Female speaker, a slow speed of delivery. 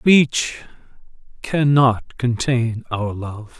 No: male; slow, 100 wpm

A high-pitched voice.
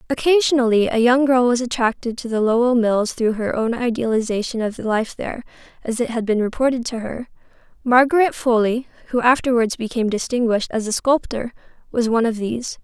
Yes: high, 235 Hz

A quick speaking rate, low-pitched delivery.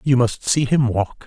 Yes: fast, 240 wpm; low, 125 Hz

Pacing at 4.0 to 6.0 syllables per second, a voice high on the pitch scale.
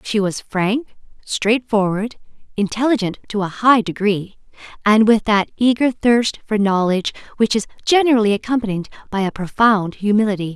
Yes: 5.0 syllables/s; high, 215 Hz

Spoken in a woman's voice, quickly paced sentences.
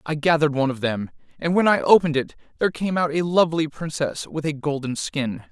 No: male; fast, 220 wpm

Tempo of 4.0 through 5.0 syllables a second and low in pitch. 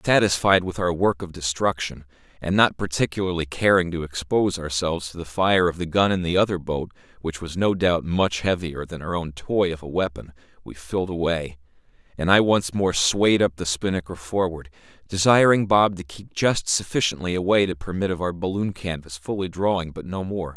No: 5.3 syllables/s; very low, 90 Hz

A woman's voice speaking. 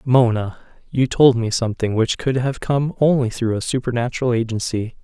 No: male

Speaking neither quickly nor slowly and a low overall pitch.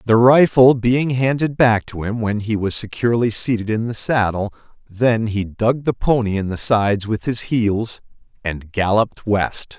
Yes: average, 180 wpm; low, 110 Hz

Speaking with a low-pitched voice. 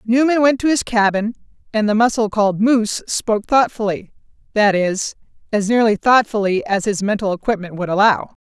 No: high, 215 Hz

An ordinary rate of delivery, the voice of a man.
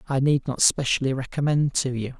Yes: average, 190 wpm; male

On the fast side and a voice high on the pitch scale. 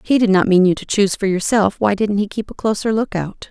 Yes: fast, 310 wpm; high, 200 Hz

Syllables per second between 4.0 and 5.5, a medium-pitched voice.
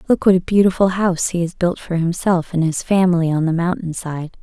No: 5.7 syllables/s; medium, 175 Hz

